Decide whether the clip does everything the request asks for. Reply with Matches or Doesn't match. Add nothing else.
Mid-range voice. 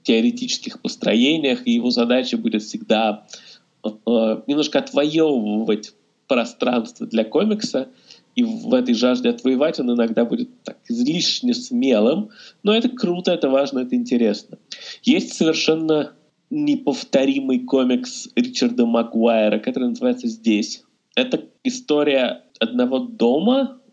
Matches